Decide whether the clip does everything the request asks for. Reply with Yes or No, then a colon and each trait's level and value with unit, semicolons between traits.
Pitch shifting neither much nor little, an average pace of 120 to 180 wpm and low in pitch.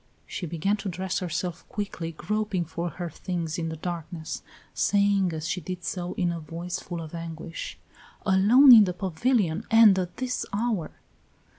No: average, 3.3 semitones; average, 165 wpm; medium, 180 Hz